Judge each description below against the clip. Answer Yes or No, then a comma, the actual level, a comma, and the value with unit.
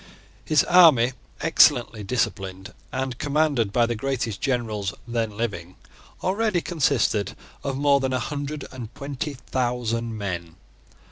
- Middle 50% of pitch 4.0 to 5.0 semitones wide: Yes, average, 4.4 semitones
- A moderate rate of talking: No, slow, 125 wpm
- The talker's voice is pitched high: No, low, 125 Hz